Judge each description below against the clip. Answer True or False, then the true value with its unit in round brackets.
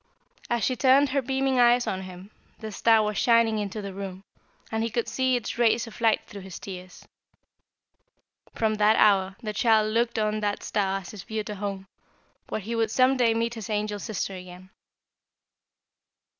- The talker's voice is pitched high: True (215 Hz)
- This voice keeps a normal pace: True (180 wpm)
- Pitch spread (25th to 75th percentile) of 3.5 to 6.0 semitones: False (2.8 semitones)